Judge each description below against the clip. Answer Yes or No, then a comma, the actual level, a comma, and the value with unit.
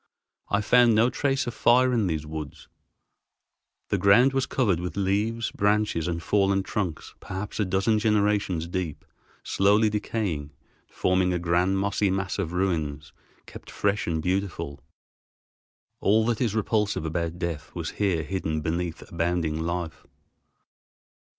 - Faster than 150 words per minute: No, slow, 135 wpm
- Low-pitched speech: Yes, very low, 95 Hz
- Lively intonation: No, average, 4.0 semitones